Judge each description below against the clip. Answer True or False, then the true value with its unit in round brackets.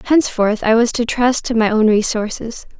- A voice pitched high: True (230 Hz)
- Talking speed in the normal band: True (195 wpm)